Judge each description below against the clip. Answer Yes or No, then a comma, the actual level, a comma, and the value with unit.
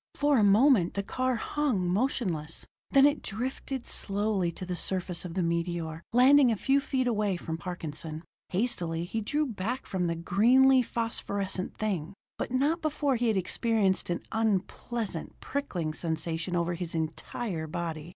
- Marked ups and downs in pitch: Yes, wide, 6.3 semitones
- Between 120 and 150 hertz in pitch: No, high, 195 Hz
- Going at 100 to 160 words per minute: Yes, average, 155 wpm